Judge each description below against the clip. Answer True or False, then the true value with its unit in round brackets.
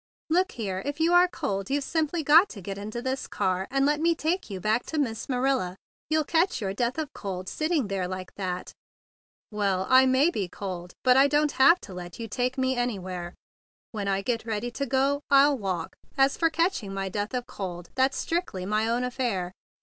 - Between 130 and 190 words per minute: False (205 wpm)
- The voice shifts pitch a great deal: True (6.6 semitones)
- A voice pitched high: True (245 Hz)